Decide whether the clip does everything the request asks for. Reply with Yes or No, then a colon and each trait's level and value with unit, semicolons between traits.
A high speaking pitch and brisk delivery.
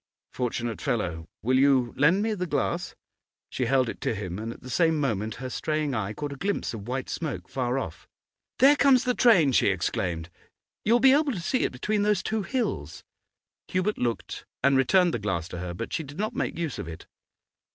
No: low, 135 Hz; fast, 210 wpm